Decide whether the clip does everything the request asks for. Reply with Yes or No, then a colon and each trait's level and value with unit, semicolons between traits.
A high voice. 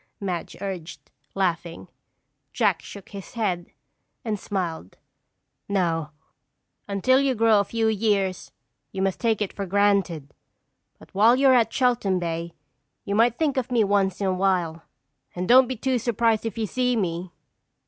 Yes: high, 200 Hz